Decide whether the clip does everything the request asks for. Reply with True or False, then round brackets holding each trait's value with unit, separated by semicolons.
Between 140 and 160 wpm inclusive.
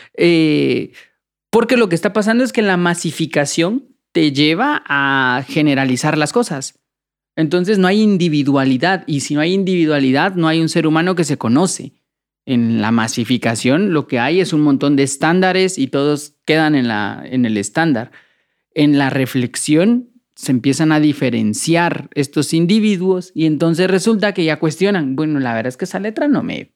False (170 wpm)